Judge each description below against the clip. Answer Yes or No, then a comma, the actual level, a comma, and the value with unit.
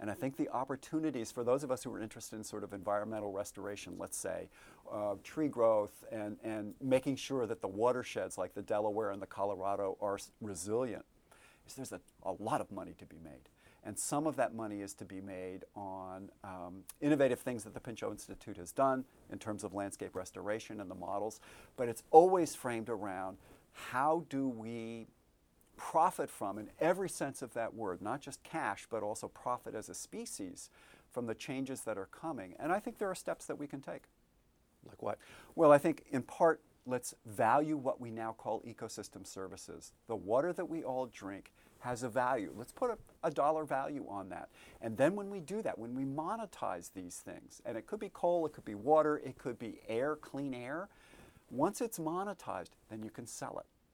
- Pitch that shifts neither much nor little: No, wide, 6.2 semitones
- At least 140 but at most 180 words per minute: No, average, 200 wpm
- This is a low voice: Yes, low, 120 Hz